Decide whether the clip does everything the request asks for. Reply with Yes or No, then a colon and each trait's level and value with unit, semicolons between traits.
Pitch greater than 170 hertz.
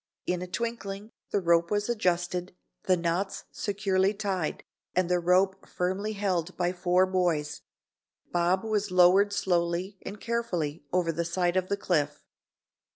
Yes: medium, 185 Hz